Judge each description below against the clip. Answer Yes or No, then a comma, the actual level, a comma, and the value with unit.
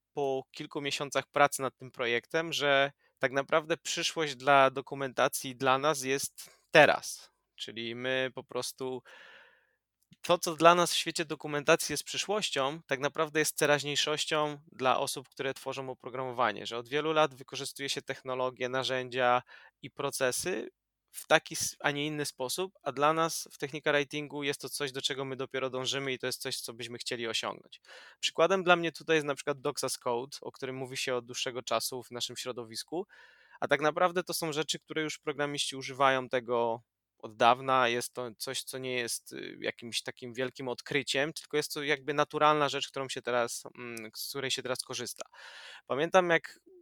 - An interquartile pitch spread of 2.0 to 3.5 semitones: Yes, average, 2.9 semitones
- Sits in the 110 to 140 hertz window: Yes, low, 135 Hz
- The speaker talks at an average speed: No, fast, 175 wpm